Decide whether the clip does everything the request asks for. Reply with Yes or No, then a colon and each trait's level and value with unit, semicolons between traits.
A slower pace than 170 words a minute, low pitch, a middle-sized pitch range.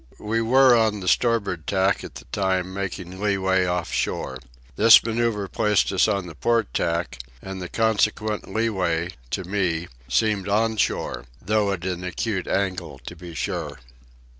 Yes: average, 160 wpm; very low, 95 Hz; average, 3.3 semitones